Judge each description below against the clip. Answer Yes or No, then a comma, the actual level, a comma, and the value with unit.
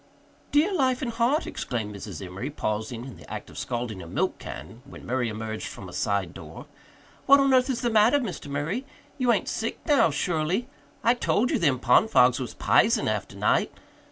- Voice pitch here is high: No, medium, 145 Hz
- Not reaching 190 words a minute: No, average, 195 wpm